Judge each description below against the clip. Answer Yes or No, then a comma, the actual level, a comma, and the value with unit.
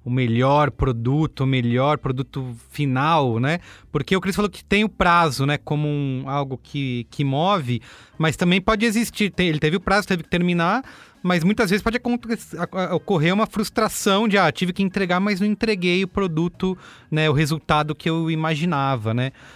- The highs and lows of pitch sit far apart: Yes, wide, 5.9 semitones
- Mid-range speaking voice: Yes, medium, 165 Hz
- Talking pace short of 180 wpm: No, fast, 185 wpm